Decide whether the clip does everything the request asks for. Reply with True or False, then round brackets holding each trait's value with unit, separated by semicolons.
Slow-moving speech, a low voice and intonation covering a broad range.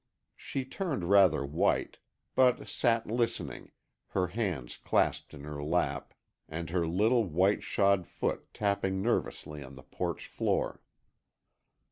True (125 wpm; 95 Hz; 6.0 semitones)